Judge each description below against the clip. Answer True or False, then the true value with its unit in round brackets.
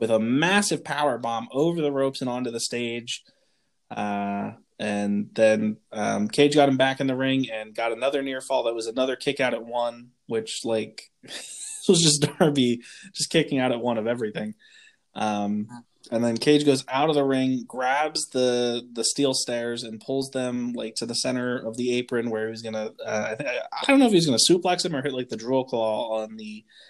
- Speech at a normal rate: False (210 wpm)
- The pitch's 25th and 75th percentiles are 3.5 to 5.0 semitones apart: True (3.8 semitones)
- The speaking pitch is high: False (125 Hz)